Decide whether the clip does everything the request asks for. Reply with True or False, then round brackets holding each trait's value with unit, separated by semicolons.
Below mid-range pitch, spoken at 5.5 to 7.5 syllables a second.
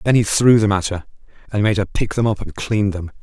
True (105 Hz; 5.8 syllables/s)